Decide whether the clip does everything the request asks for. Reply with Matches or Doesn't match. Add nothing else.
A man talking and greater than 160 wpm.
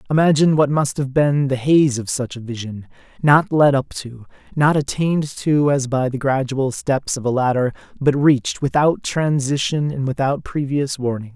Matches